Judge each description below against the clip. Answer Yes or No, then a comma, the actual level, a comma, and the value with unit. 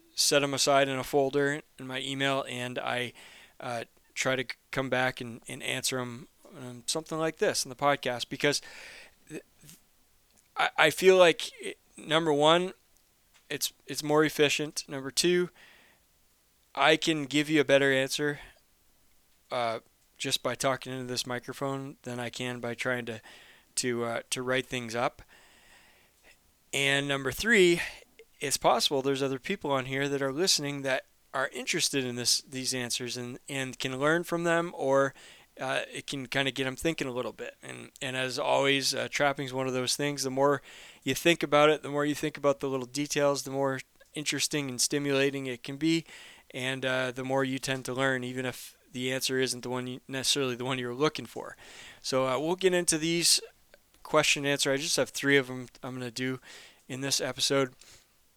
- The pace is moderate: Yes, average, 190 wpm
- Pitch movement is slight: Yes, narrow, 2.2 semitones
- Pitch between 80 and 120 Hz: No, low, 135 Hz